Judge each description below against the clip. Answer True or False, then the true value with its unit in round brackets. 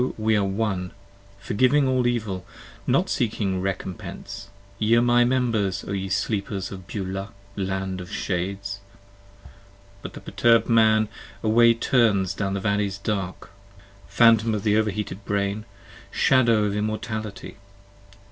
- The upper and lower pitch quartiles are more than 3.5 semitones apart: False (2.8 semitones)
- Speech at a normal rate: False (130 wpm)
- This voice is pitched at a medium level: False (105 Hz)